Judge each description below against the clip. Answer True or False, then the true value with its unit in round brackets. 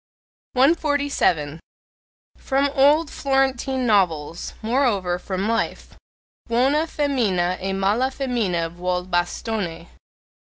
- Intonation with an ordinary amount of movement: False (7.0 semitones)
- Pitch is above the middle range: True (225 Hz)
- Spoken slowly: True (85 wpm)